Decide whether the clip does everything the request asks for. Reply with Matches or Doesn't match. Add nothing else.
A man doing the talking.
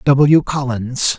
Matches